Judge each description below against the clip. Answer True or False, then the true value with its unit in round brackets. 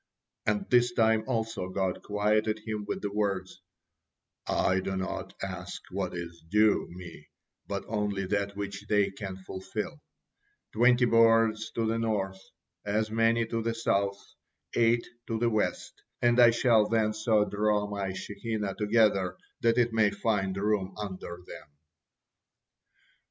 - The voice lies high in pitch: False (105 Hz)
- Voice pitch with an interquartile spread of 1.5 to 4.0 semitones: True (2.5 semitones)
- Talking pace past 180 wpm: False (140 wpm)